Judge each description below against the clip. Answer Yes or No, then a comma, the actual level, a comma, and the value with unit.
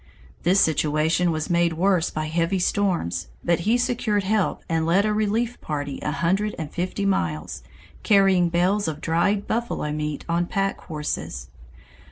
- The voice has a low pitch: No, medium, 175 Hz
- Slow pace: No, average, 155 wpm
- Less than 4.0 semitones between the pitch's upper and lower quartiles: No, average, 4.4 semitones